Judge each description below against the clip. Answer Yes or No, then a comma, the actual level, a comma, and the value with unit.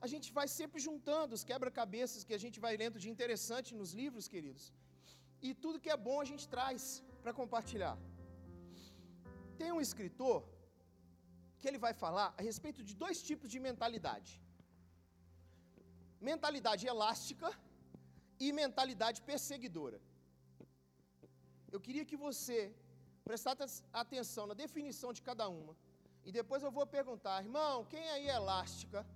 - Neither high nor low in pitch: No, high, 225 Hz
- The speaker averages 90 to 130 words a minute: No, fast, 140 wpm